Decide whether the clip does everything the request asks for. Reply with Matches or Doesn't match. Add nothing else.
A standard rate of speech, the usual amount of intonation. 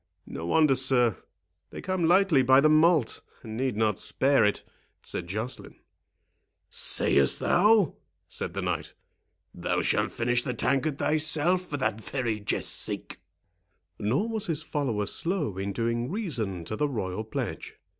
Doesn't match